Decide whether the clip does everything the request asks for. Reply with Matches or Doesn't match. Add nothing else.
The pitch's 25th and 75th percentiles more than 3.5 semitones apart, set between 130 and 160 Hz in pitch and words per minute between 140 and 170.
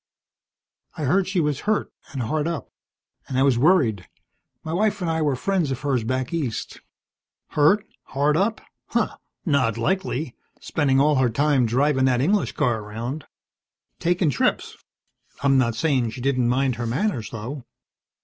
Matches